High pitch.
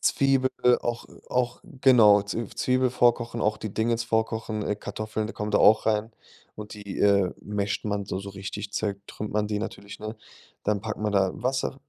No: low, 105 Hz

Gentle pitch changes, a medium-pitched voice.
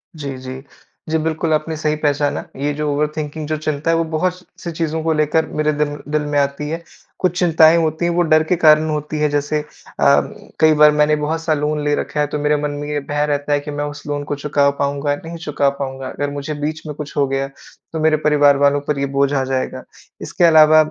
Yes: narrow, 1.5 semitones; medium, 150 Hz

